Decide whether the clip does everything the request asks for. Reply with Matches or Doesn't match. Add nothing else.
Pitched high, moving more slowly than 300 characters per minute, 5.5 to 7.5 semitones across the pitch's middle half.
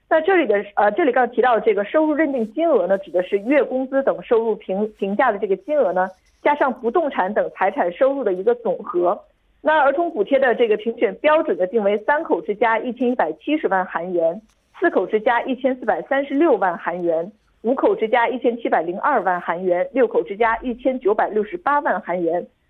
Doesn't match